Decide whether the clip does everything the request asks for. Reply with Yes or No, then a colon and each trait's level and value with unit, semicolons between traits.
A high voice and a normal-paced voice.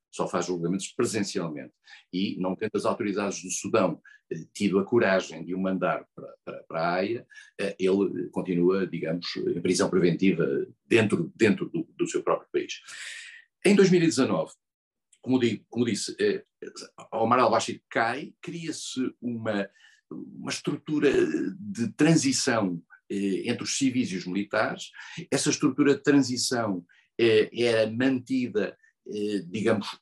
No: low, 120 Hz; average, 140 wpm